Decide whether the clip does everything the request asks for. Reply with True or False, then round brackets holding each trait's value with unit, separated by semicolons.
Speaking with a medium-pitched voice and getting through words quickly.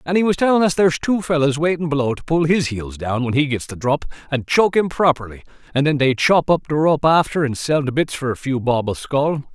True (145 Hz; 265 wpm)